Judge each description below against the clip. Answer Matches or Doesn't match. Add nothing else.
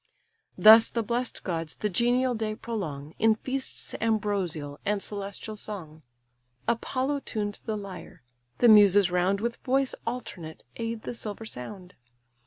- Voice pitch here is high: Matches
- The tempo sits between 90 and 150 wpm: Matches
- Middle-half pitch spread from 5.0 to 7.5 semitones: Doesn't match